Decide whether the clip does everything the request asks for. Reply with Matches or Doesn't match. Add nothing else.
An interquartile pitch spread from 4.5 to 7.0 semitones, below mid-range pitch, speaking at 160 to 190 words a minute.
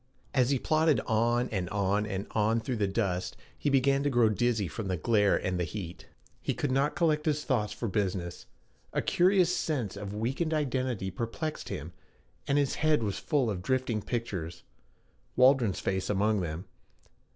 Matches